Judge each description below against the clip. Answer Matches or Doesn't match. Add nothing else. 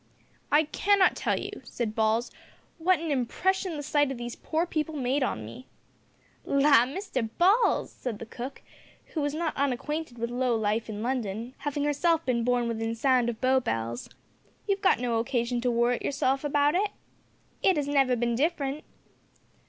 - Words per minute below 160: Doesn't match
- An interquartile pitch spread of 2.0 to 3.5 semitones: Doesn't match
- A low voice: Doesn't match